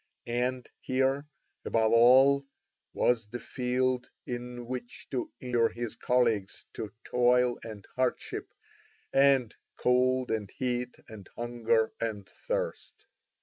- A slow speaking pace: Yes, slow, 110 wpm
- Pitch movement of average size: No, narrow, 1.8 semitones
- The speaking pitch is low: Yes, low, 125 Hz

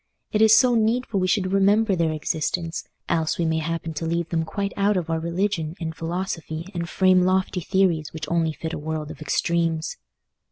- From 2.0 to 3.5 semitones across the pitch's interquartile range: Yes, average, 3.1 semitones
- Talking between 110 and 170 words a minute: No, average, 195 wpm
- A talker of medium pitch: Yes, medium, 170 Hz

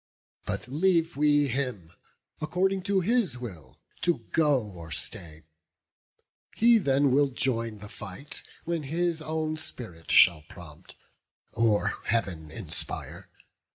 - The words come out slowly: Yes, slow, 120 wpm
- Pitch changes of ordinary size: No, wide, 7.9 semitones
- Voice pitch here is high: No, low, 135 Hz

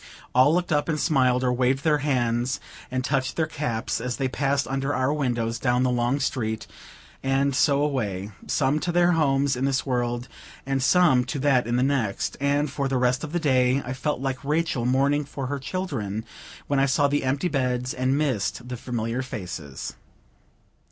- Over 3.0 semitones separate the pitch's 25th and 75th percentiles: No, narrow, 2.4 semitones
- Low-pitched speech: Yes, low, 130 Hz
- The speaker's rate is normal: Yes, average, 190 wpm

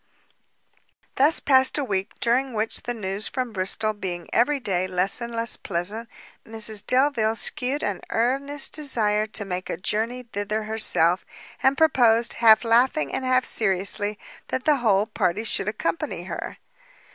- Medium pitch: No, high, 220 Hz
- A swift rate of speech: No, average, 150 wpm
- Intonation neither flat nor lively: Yes, average, 4.0 semitones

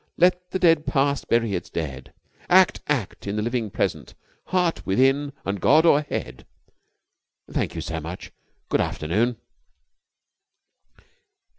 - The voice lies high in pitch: No, low, 125 Hz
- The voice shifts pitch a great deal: Yes, wide, 8.4 semitones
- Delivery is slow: Yes, slow, 125 wpm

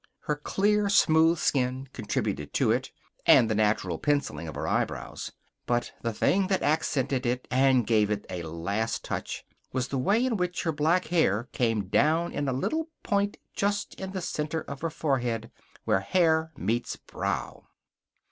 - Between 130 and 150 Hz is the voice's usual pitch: Yes, medium, 140 Hz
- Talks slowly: No, average, 165 wpm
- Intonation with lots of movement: Yes, wide, 7.0 semitones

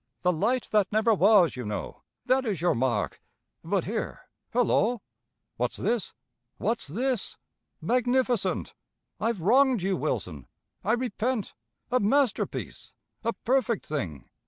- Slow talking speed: Yes, slow, 125 wpm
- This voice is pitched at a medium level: No, high, 215 Hz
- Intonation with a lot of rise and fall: Yes, wide, 6.0 semitones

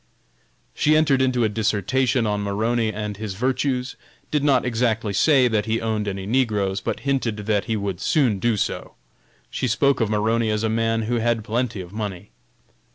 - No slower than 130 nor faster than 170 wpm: No, average, 180 wpm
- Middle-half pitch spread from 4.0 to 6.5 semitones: No, average, 3.2 semitones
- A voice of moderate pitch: No, low, 110 Hz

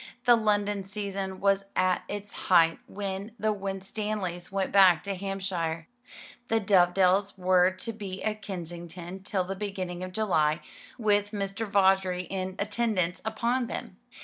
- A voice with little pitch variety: Yes, narrow, 2.1 semitones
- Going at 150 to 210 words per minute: No, average, 140 wpm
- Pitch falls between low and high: No, high, 195 Hz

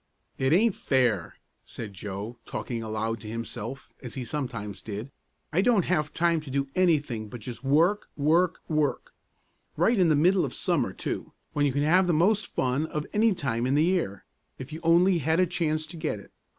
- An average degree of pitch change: No, wide, 6.3 semitones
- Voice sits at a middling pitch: Yes, medium, 150 Hz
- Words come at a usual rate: Yes, average, 195 wpm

